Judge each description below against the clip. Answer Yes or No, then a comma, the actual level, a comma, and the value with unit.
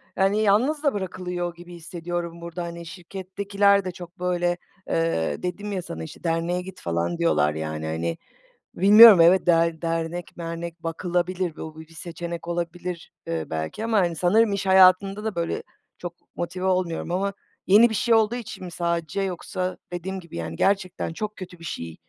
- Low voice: No, medium, 175 Hz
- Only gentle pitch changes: Yes, narrow, 2.3 semitones